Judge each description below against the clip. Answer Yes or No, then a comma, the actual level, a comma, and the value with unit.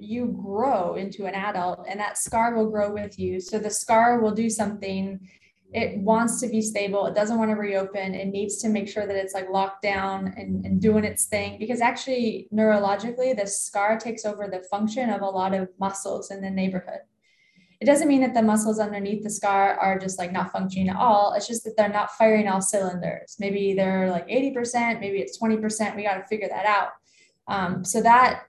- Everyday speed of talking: No, fast, 210 wpm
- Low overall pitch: No, high, 205 Hz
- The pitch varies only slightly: Yes, narrow, 2.2 semitones